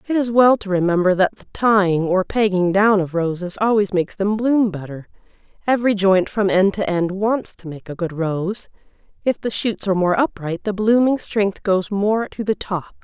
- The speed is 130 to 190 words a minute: No, fast, 205 wpm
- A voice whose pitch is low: No, high, 200 Hz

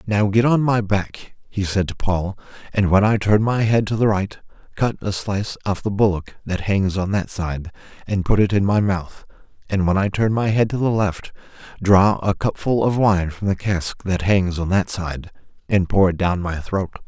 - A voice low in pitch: Yes, low, 100 Hz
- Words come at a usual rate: No, fast, 220 wpm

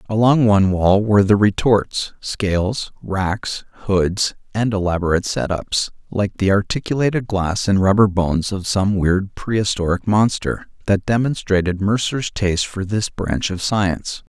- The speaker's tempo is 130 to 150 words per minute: Yes, average, 140 wpm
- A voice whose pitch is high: No, low, 100 Hz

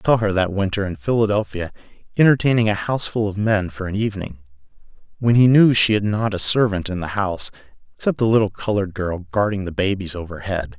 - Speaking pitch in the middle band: No, low, 100 Hz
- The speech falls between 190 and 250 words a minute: Yes, average, 195 wpm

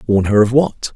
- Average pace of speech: No, fast, 250 wpm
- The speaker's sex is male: Yes, male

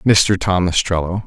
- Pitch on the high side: No, very low, 90 Hz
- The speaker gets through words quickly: No, average, 140 wpm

